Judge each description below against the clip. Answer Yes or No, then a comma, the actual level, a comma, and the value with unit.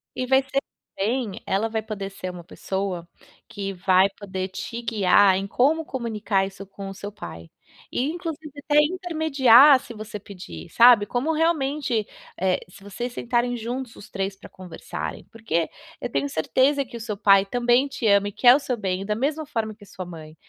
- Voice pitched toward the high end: Yes, high, 220 Hz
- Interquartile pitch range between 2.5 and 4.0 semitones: No, average, 5.1 semitones